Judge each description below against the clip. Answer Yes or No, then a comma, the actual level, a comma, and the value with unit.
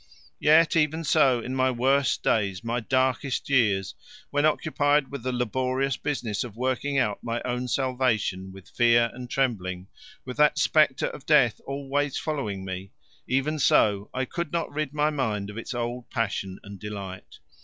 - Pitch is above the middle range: No, low, 125 Hz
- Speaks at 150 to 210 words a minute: Yes, average, 165 wpm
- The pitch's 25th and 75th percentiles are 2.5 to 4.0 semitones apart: No, average, 4.6 semitones